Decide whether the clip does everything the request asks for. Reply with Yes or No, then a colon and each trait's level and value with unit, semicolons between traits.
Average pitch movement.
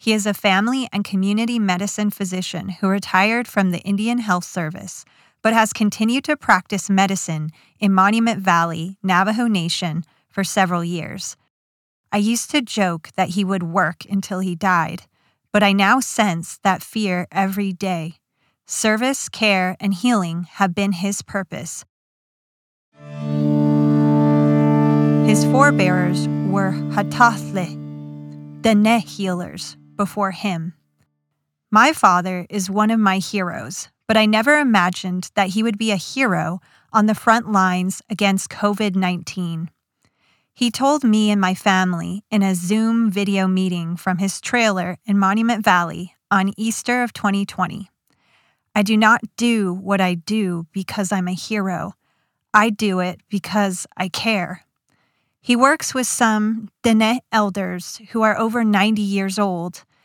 Yes: average, 3.4 semitones